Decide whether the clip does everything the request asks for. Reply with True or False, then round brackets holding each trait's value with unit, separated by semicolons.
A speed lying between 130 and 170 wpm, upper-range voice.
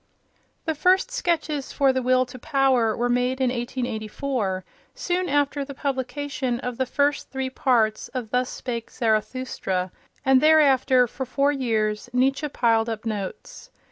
True (145 wpm; 255 Hz)